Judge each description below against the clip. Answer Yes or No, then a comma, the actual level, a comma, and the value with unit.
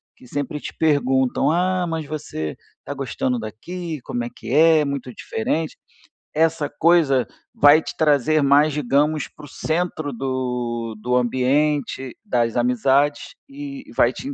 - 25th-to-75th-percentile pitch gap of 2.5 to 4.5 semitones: Yes, average, 3.9 semitones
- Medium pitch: Yes, medium, 145 Hz